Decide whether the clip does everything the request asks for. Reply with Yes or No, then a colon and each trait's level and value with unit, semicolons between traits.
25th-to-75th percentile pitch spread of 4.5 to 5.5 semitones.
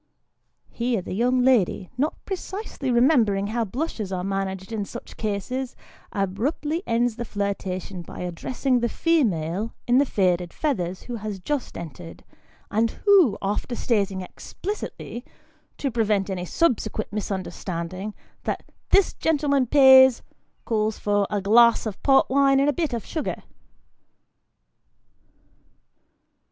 Yes: average, 5.2 semitones